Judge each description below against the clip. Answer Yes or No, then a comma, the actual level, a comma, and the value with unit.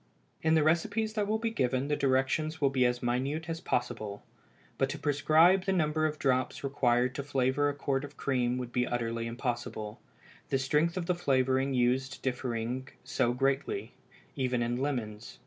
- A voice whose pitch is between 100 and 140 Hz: Yes, low, 135 Hz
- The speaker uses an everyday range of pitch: Yes, average, 3.8 semitones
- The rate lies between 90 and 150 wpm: No, average, 175 wpm